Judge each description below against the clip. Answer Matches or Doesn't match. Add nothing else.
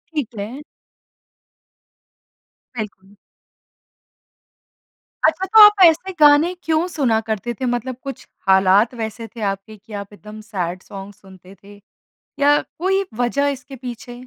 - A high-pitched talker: Matches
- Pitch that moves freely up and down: Matches